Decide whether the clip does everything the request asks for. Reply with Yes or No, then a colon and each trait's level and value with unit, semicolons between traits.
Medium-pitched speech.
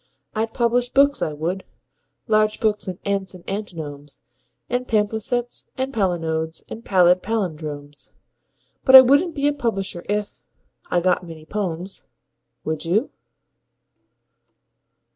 No: high, 200 Hz